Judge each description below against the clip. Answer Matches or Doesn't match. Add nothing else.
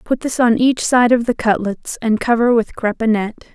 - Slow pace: Doesn't match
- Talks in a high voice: Matches